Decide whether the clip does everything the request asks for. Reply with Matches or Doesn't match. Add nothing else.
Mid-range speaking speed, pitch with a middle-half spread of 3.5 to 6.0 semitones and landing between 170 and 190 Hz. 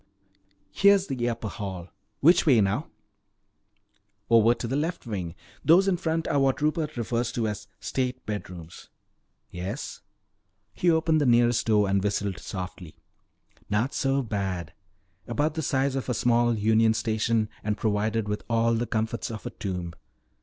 Doesn't match